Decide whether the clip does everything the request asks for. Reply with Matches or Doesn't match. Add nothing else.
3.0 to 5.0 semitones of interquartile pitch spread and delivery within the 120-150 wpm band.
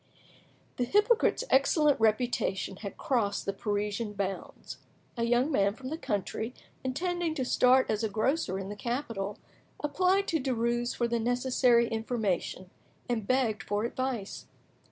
Matches